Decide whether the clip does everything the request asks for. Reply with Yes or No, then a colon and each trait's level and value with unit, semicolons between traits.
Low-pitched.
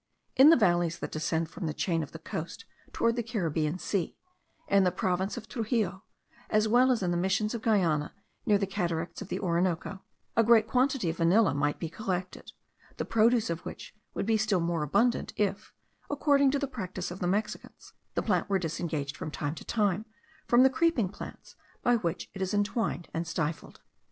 No: high, 190 Hz